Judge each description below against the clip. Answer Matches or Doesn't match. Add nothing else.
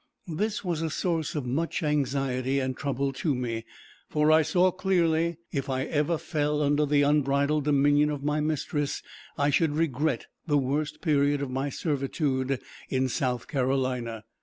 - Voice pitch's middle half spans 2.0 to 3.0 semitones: Matches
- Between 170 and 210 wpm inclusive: Doesn't match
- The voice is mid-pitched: Matches